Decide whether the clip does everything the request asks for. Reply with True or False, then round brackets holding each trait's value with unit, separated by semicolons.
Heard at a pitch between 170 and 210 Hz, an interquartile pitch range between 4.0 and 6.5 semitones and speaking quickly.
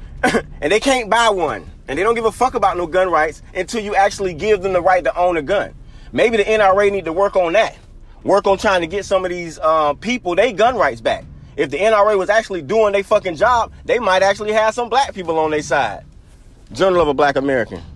True (190 Hz; 4.7 semitones; 240 wpm)